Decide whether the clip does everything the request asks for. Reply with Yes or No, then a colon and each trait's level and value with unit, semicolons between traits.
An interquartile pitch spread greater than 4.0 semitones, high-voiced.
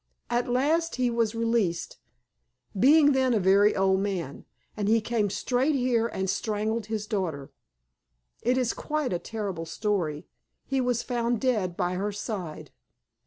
Yes: average, 4.4 semitones; high, 220 Hz